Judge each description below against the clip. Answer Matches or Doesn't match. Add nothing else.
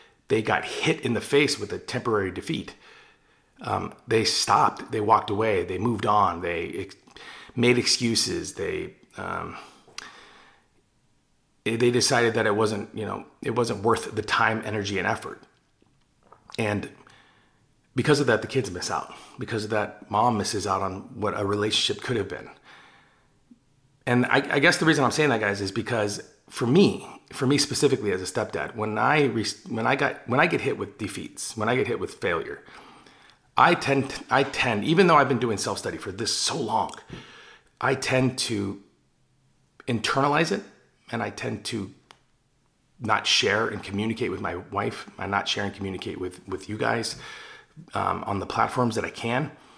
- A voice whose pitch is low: Matches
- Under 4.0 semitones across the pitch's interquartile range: Doesn't match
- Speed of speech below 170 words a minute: Doesn't match